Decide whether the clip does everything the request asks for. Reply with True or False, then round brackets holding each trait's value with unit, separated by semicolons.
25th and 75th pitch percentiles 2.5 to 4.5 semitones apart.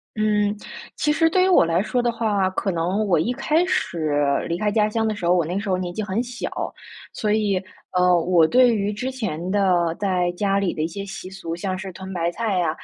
True (3.4 semitones)